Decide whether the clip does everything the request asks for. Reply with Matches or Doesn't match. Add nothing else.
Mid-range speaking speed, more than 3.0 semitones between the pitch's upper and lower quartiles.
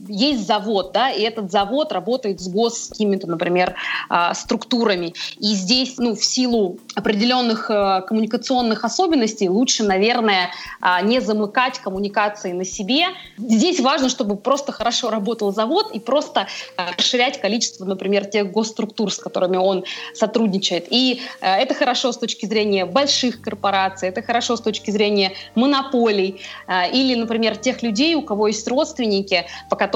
Matches